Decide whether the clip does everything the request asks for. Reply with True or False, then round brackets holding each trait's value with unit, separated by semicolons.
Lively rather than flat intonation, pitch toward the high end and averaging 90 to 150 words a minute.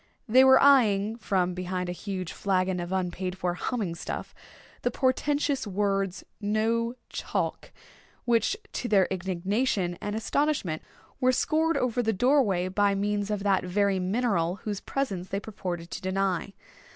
False (4.0 semitones; 200 Hz; 145 wpm)